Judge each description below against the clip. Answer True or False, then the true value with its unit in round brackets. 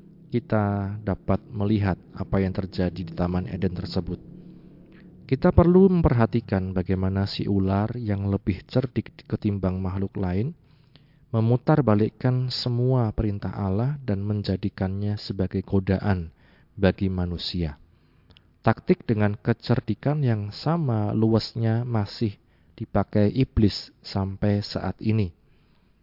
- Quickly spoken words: False (105 wpm)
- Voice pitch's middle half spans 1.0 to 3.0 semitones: False (4.3 semitones)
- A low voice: True (105 Hz)